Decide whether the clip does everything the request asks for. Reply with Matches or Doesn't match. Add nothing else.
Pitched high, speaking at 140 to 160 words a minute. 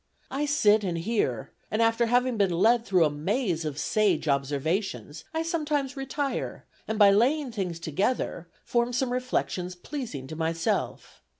Matches